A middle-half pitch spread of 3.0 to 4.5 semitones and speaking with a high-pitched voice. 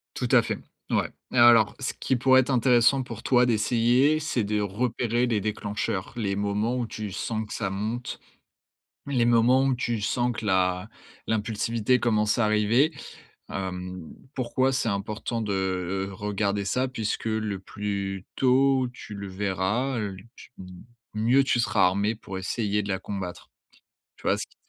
No: average, 3.4 semitones; low, 110 Hz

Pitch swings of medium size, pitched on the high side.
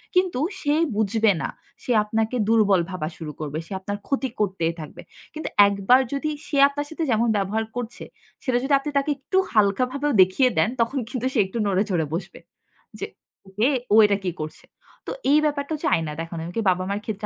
No: wide, 6.4 semitones; high, 220 Hz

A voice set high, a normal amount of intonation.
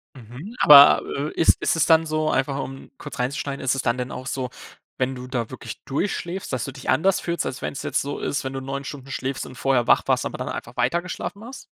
No: low, 135 Hz; average, 3.2 semitones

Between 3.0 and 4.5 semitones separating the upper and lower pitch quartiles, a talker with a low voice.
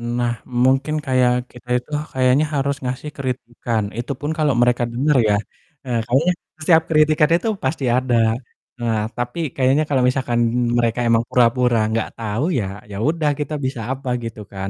Yes: average, 3.3 semitones; low, 130 Hz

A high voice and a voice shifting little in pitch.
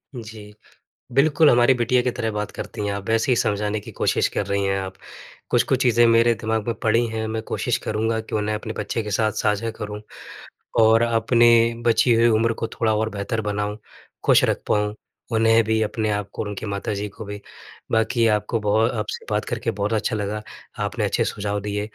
No: low, 110 Hz; narrow, 1.7 semitones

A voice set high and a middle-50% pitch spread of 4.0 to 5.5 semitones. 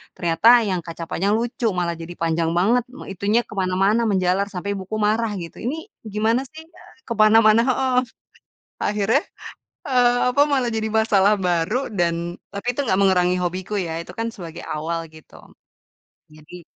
Yes: high, 200 Hz; average, 4.3 semitones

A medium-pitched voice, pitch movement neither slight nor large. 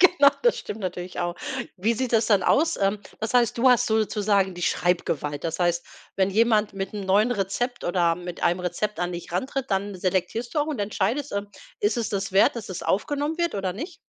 No: high, 205 Hz; average, 4.7 semitones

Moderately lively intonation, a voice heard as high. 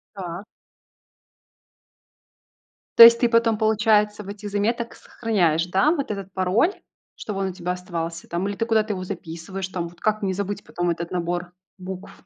Yes: average, 3.3 semitones; high, 195 Hz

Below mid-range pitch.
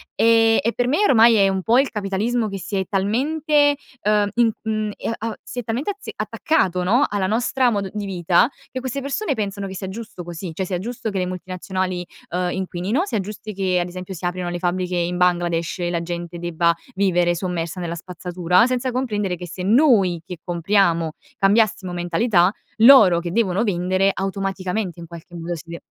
No: high, 190 Hz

